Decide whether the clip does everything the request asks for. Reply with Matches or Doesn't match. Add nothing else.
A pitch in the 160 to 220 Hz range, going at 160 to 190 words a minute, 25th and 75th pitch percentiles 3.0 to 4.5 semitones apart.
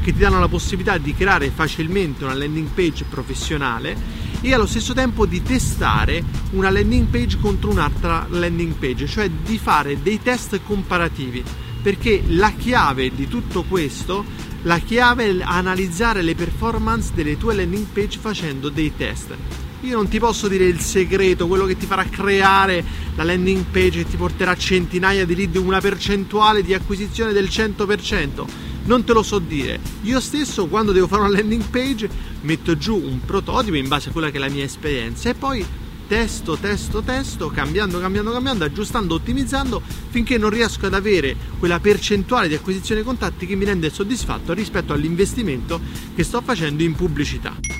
Doesn't match